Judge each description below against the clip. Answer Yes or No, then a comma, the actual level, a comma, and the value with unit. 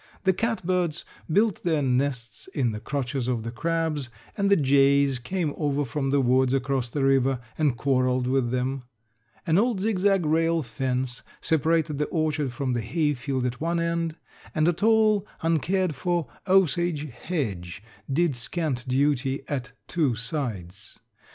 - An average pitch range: Yes, average, 4.7 semitones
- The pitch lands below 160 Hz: Yes, medium, 140 Hz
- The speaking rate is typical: Yes, average, 150 wpm